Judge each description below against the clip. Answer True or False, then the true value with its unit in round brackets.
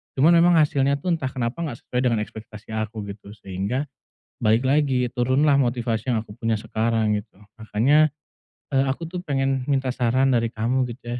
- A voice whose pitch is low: True (125 Hz)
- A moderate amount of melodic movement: True (3.5 semitones)